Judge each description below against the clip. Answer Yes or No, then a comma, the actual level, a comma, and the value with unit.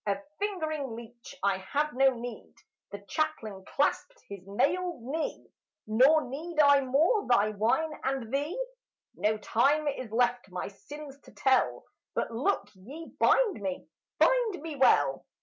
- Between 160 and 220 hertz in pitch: No, very high, 270 Hz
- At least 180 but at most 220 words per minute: No, average, 145 wpm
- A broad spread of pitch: Yes, wide, 6.1 semitones